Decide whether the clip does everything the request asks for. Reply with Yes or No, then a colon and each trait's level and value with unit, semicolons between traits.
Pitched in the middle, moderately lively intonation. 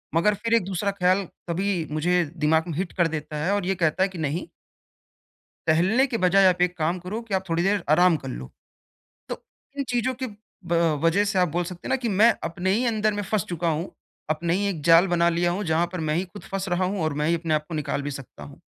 Yes: medium, 180 Hz; average, 3.2 semitones